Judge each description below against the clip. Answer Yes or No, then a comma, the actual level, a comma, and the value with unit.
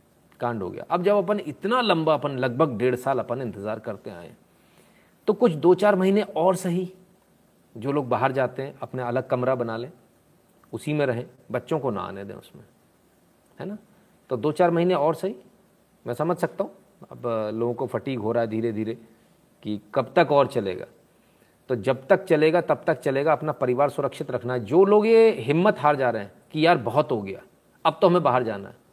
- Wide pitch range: Yes, wide, 6.9 semitones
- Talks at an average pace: No, fast, 205 wpm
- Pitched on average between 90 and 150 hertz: Yes, medium, 145 Hz